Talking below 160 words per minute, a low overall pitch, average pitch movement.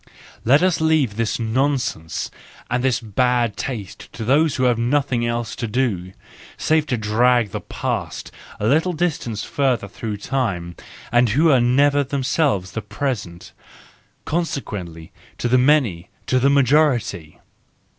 Yes: slow, 135 wpm; low, 125 Hz; average, 4.7 semitones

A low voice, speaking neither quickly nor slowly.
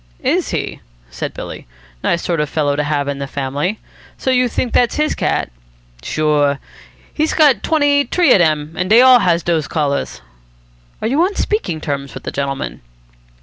No: medium, 165 Hz; average, 180 wpm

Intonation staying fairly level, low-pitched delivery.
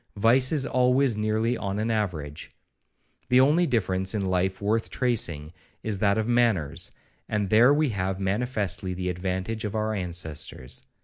No: average, 4.3 semitones; low, 105 Hz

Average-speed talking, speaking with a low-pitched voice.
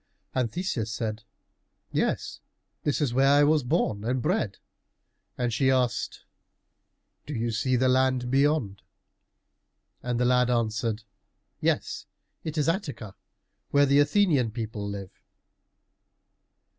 No: slow, 120 wpm; low, 125 Hz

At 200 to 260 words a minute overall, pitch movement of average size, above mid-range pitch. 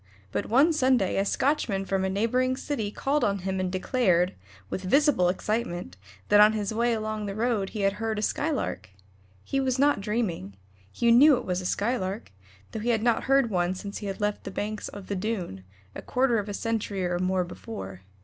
Yes: fast, 205 wpm; average, 4.1 semitones; high, 210 Hz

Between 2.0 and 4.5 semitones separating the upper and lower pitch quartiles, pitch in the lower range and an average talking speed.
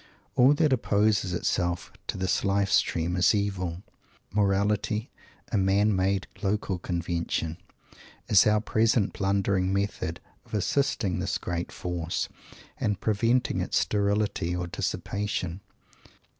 No: average, 2.7 semitones; low, 100 Hz; slow, 115 wpm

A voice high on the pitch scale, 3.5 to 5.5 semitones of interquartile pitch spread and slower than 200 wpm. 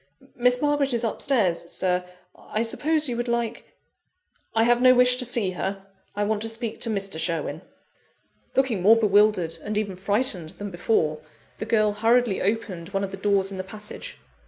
Yes: high, 215 Hz; average, 3.8 semitones; average, 180 wpm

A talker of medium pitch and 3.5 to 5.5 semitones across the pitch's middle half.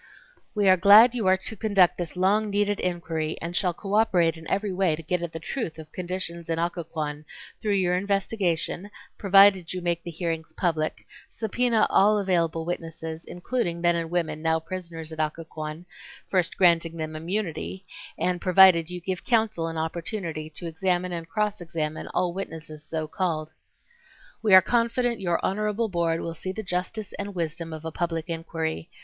No: medium, 175 Hz; average, 3.1 semitones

